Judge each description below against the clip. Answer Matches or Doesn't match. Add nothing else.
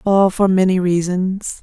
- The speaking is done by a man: Doesn't match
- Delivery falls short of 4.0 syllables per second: Matches